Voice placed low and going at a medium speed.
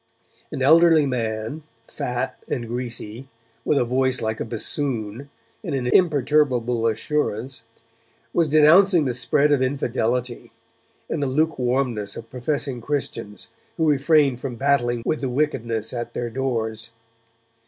No: low, 130 Hz; slow, 130 wpm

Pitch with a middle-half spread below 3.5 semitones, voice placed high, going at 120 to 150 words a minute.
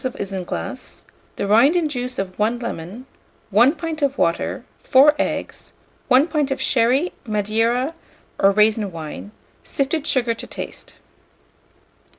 No: average, 5.1 semitones; high, 240 Hz; slow, 135 wpm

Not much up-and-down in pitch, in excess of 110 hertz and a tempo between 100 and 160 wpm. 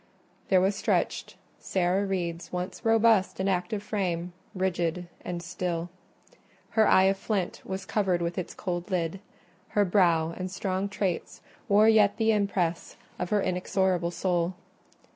Yes: narrow, 2.2 semitones; medium, 185 Hz; average, 145 wpm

